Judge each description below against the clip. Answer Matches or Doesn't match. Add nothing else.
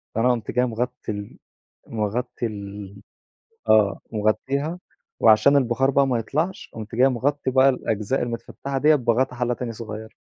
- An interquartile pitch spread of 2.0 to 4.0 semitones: Matches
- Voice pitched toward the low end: Matches